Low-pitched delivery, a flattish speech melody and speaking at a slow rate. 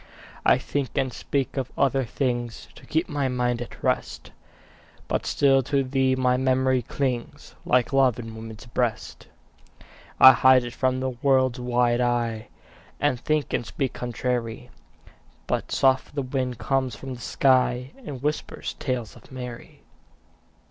No: low, 130 Hz; narrow, 1.7 semitones; average, 150 wpm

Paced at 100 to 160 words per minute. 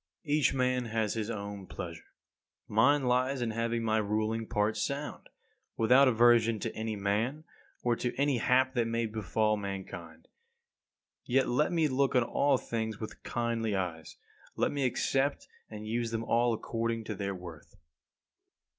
Yes: average, 155 wpm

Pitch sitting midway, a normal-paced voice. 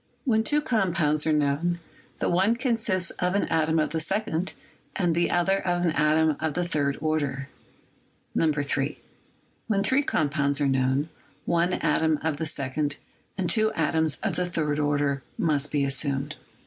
Yes: medium, 160 Hz; average, 160 wpm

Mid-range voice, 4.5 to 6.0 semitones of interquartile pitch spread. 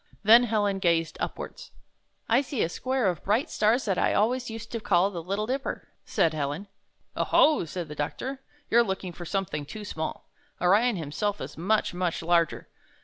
No: high, 200 Hz; average, 5.2 semitones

